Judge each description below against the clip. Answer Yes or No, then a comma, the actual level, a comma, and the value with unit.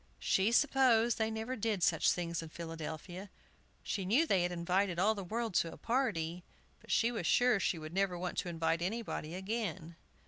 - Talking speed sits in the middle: Yes, average, 185 wpm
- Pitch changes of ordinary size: Yes, average, 4.8 semitones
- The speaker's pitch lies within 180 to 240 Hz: Yes, high, 190 Hz